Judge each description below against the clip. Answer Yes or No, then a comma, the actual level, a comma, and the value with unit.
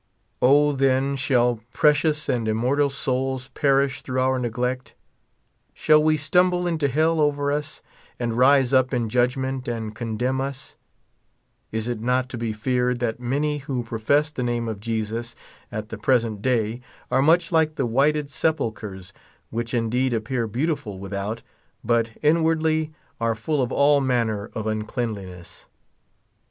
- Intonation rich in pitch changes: No, average, 3.8 semitones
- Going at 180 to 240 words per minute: No, average, 145 wpm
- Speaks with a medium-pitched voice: No, low, 125 Hz